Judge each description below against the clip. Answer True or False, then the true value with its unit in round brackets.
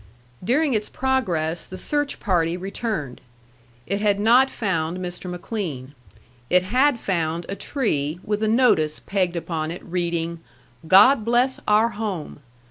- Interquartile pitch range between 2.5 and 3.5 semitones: False (5.3 semitones)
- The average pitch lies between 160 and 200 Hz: True (190 Hz)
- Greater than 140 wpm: False (135 wpm)